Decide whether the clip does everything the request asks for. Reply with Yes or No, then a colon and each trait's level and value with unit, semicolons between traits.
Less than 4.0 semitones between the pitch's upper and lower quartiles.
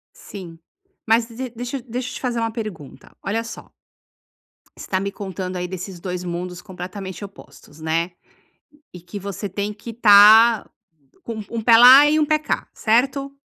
No: average, 4.3 semitones